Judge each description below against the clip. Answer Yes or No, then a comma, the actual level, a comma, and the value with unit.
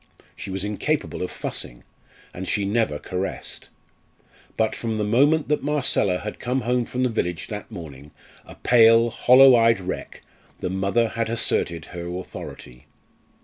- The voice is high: No, low, 110 Hz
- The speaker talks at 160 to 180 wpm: No, average, 150 wpm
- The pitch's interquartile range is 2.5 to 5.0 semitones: Yes, average, 4.7 semitones